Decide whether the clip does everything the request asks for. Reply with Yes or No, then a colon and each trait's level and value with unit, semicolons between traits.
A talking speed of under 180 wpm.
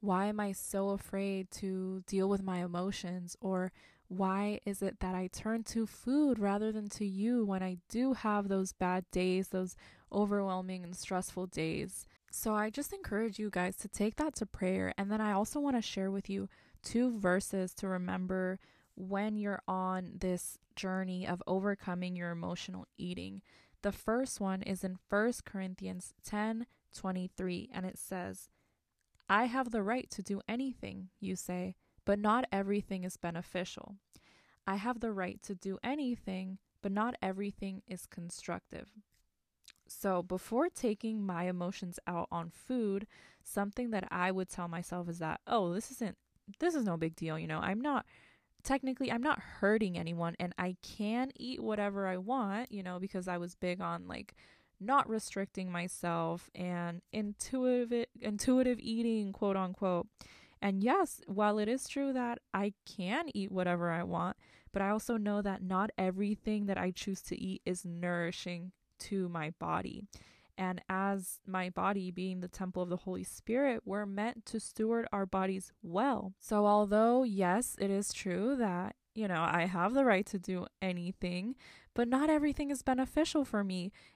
Yes: average, 170 wpm